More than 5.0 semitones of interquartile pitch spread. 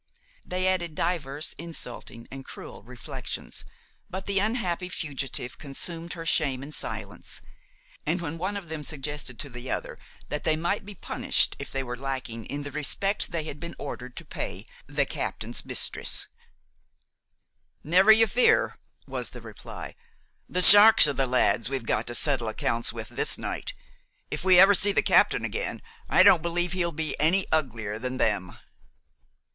Yes: wide, 5.6 semitones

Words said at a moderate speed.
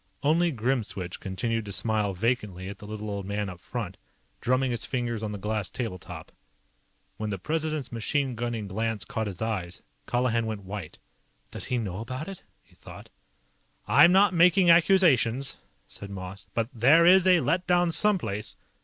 Yes: average, 170 wpm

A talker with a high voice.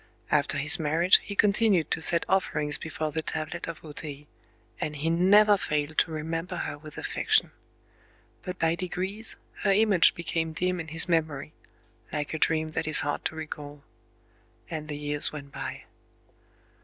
No: medium, 160 Hz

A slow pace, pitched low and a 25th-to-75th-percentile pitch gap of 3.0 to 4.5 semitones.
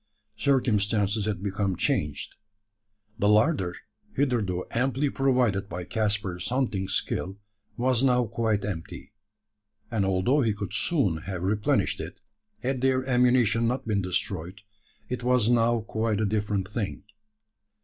Yes: slow, 130 wpm; low, 110 Hz; average, 4.2 semitones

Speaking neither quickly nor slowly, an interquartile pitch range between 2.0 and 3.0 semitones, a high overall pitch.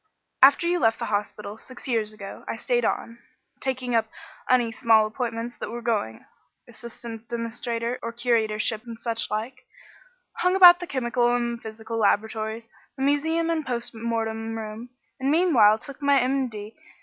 Yes: average, 155 wpm; average, 2.7 semitones; high, 235 Hz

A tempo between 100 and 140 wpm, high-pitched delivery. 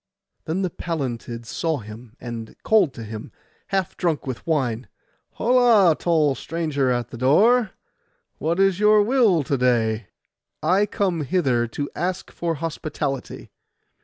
No: slow, 135 wpm; medium, 155 Hz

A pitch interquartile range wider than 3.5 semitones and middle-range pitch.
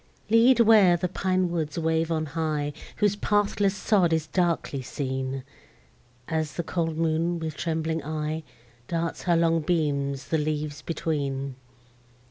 No: narrow, 2.5 semitones; medium, 160 Hz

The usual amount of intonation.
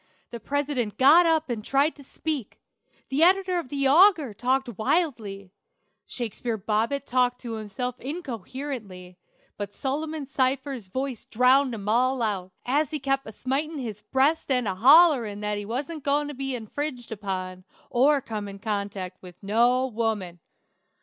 Yes: average, 5.0 semitones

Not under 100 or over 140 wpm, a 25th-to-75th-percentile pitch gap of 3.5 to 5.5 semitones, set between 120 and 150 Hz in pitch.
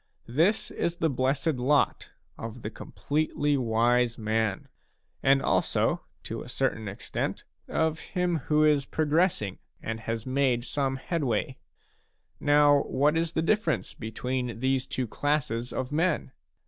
Yes: slow, 135 wpm; average, 4.3 semitones; low, 135 Hz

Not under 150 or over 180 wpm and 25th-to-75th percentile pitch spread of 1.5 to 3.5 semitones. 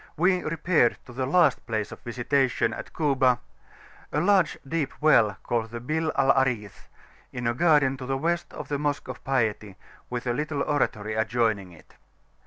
No: average, 175 wpm; average, 4.4 semitones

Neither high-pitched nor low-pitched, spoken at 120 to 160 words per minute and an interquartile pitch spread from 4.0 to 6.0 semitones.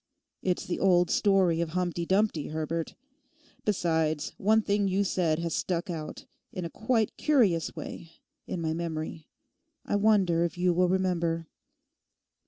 No: medium, 175 Hz; average, 145 wpm; average, 2.8 semitones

